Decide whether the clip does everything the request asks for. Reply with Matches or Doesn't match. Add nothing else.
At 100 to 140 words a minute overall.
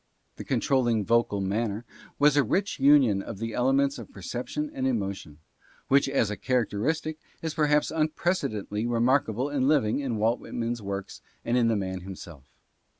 Doesn't match